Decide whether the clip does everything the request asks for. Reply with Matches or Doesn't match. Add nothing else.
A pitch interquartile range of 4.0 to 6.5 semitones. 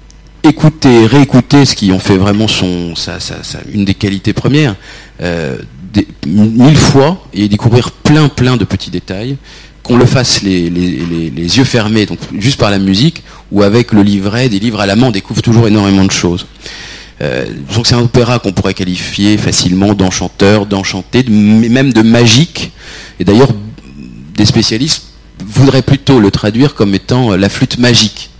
Matches